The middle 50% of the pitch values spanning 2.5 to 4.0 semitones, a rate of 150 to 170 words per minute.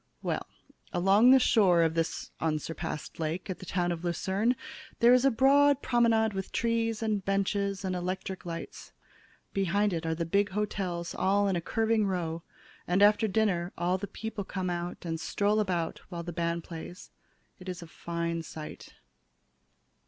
Yes: average, 3.6 semitones; average, 165 wpm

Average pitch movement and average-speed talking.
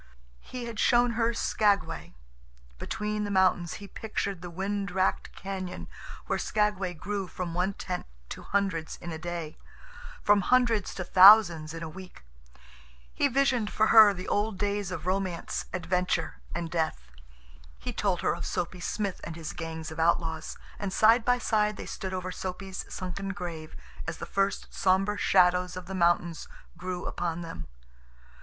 Yes: average, 3.0 semitones; average, 160 wpm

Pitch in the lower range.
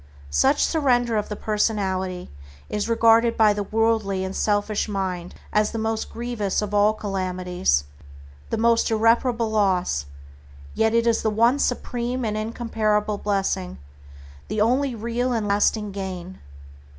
No: high, 215 Hz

